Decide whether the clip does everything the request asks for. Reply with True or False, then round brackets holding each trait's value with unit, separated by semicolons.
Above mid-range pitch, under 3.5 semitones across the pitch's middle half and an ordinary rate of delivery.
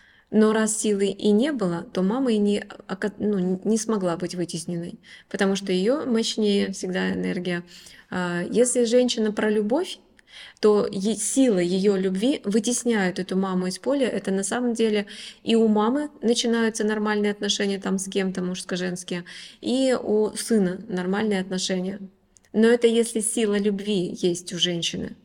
True (205 Hz; 3.1 semitones; 145 wpm)